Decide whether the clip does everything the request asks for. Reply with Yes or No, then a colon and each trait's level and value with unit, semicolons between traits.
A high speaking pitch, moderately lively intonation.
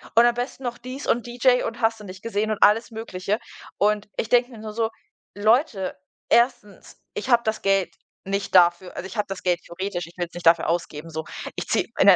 Yes: high, 210 Hz; average, 4.3 semitones